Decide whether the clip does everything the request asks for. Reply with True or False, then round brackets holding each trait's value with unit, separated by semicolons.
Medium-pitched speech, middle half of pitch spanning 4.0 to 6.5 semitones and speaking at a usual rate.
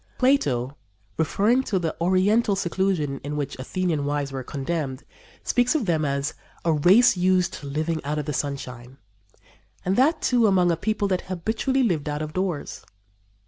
True (170 Hz; 5.4 semitones; 165 wpm)